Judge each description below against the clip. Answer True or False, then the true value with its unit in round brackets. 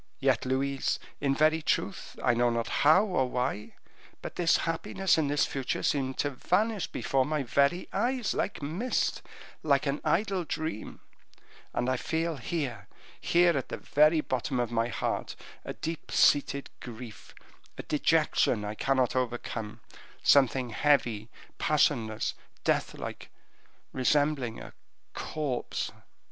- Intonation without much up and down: False (4.4 semitones)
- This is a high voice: False (140 Hz)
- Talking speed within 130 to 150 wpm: True (135 wpm)